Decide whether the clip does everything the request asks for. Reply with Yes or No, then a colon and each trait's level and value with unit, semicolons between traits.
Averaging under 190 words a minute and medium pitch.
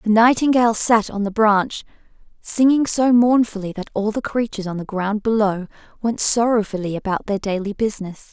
No: average, 165 wpm; high, 215 Hz